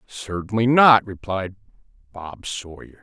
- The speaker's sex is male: Yes, male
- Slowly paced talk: Yes, slow, 100 wpm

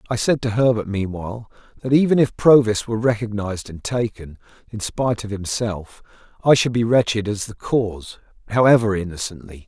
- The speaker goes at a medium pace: Yes, average, 160 wpm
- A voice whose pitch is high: No, low, 110 Hz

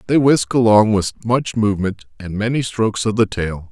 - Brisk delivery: No, average, 195 wpm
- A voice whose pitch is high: No, low, 110 Hz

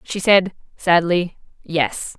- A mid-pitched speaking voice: Yes, medium, 175 Hz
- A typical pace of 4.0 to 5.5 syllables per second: No, 3.1 syllables/s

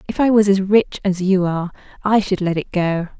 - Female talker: Yes, female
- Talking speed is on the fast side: Yes, fast, 245 wpm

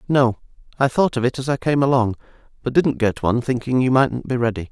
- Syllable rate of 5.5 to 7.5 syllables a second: Yes, 5.9 syllables/s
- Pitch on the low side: Yes, low, 125 Hz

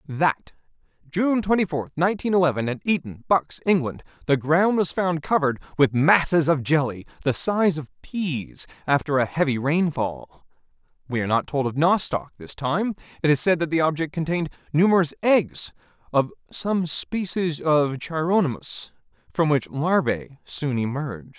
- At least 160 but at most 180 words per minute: No, average, 150 wpm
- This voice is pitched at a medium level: Yes, medium, 150 Hz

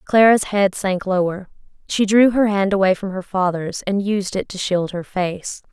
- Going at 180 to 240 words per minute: Yes, average, 200 wpm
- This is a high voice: Yes, high, 195 Hz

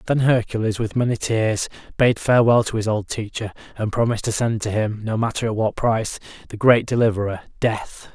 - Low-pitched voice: Yes, low, 110 Hz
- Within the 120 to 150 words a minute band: No, average, 190 wpm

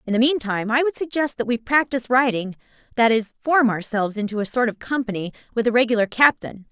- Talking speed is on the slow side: No, average, 195 wpm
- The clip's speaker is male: No, female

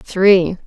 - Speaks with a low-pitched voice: No, high, 190 Hz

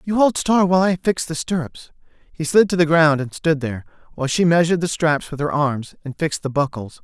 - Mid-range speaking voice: Yes, medium, 160 Hz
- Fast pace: Yes, fast, 240 wpm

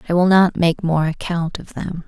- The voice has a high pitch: No, medium, 170 Hz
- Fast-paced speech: Yes, fast, 230 wpm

